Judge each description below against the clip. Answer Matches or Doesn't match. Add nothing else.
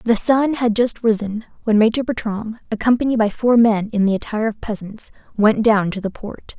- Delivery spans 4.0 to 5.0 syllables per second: Doesn't match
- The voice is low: Doesn't match